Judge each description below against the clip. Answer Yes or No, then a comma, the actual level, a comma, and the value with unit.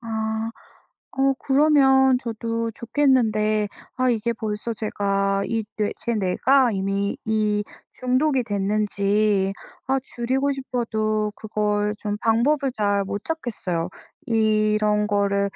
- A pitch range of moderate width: Yes, average, 3.2 semitones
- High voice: Yes, high, 220 Hz